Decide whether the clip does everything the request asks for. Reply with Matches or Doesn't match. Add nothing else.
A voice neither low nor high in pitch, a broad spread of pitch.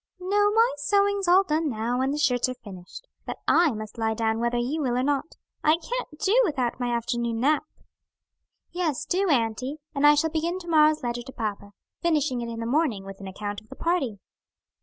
Doesn't match